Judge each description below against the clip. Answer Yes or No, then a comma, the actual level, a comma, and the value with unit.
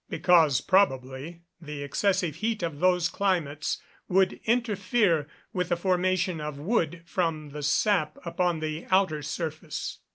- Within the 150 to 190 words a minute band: No, slow, 135 wpm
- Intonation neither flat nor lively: Yes, average, 3.5 semitones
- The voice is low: No, medium, 170 Hz